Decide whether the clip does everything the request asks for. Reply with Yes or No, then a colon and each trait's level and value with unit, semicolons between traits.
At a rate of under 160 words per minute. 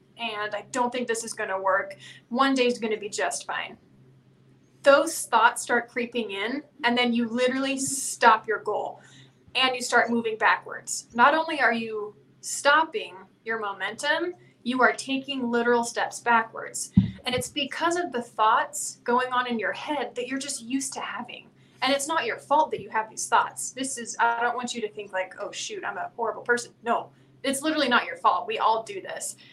No: average, 195 wpm